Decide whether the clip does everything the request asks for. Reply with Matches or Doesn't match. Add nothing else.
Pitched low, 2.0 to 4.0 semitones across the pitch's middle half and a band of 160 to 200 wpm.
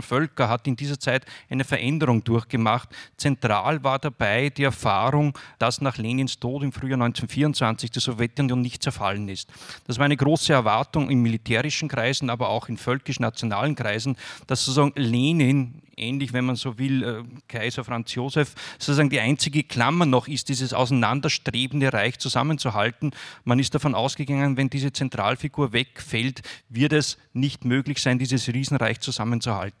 Doesn't match